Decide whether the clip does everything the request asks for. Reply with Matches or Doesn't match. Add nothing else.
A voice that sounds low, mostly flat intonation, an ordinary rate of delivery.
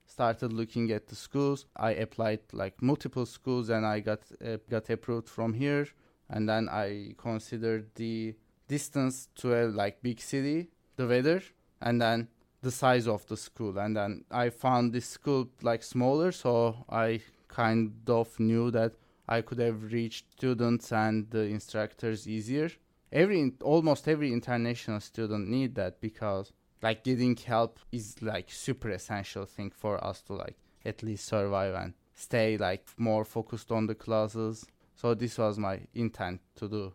Matches